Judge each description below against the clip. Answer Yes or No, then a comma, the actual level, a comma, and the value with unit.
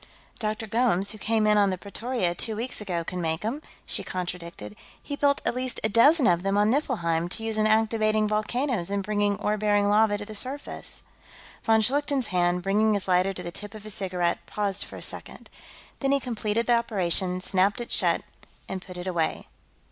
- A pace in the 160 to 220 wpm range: Yes, average, 200 wpm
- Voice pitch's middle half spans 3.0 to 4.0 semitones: Yes, average, 3.4 semitones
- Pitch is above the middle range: Yes, high, 210 Hz